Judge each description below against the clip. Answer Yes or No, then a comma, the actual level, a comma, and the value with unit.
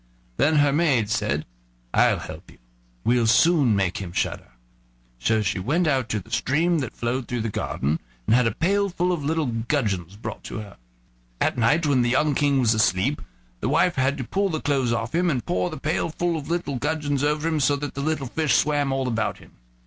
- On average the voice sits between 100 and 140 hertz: Yes, low, 135 Hz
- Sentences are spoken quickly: Yes, fast, 215 wpm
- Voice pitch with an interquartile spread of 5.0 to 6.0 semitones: Yes, average, 5.3 semitones